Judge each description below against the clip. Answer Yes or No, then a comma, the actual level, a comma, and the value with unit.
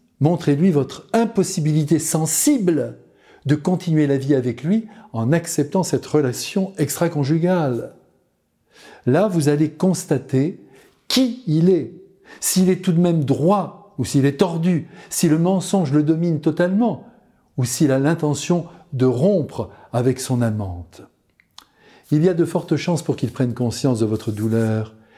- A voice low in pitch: No, medium, 155 Hz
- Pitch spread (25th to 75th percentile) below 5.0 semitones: No, average, 5.3 semitones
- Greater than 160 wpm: No, slow, 145 wpm